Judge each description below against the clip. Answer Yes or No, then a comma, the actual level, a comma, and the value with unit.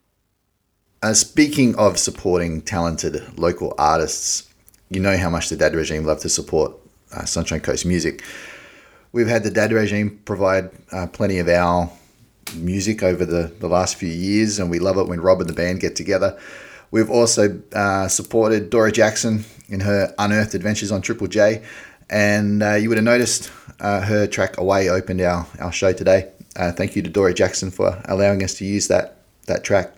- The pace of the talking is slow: No, average, 180 wpm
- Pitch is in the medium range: No, low, 100 Hz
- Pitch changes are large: No, average, 2.8 semitones